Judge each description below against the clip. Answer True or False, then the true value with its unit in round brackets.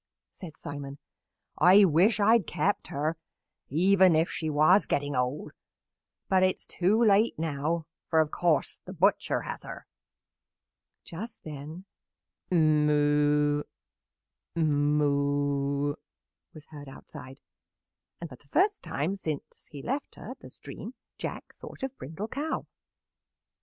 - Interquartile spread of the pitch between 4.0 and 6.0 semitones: True (4.5 semitones)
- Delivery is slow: True (130 wpm)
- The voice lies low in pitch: False (155 Hz)